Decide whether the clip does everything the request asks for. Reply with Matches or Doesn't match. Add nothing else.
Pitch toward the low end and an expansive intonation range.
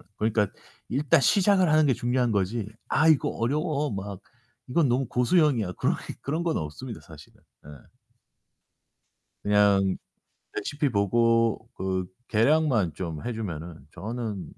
Matches